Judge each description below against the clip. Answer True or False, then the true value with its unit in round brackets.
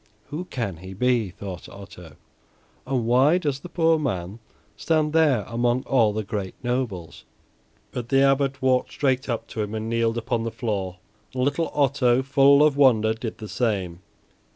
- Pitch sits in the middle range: False (120 Hz)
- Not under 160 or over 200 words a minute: True (170 wpm)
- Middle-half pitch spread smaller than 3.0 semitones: False (4.4 semitones)